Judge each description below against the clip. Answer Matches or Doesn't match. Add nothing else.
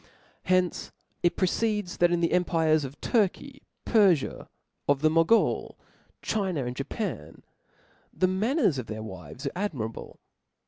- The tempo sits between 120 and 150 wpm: Matches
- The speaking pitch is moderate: Matches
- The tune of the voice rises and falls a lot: Matches